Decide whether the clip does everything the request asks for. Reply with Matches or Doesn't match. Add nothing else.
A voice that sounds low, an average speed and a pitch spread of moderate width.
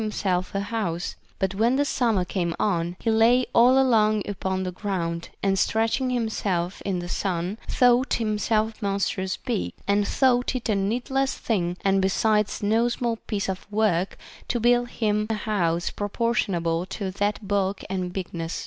Doesn't match